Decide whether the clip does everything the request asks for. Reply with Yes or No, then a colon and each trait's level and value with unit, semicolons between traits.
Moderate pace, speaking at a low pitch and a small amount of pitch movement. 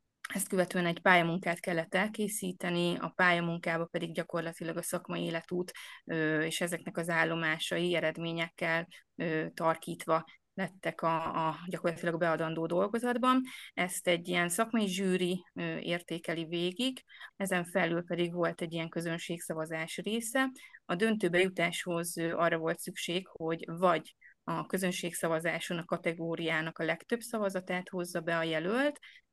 No: average, 120 wpm; medium, 175 Hz; narrow, 1.9 semitones